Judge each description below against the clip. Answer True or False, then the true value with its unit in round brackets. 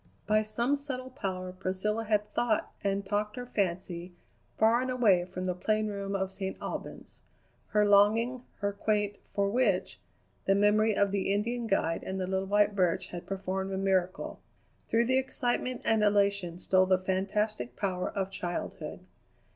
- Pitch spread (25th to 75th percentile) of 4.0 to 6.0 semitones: False (2.4 semitones)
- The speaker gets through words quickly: False (165 wpm)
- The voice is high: True (200 Hz)